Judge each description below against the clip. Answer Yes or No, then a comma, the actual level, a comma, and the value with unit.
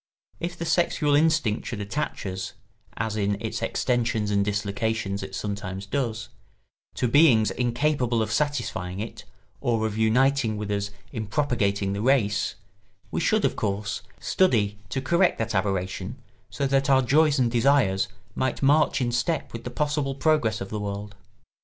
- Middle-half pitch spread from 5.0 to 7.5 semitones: Yes, average, 5.3 semitones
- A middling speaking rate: Yes, average, 160 wpm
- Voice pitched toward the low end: Yes, low, 115 Hz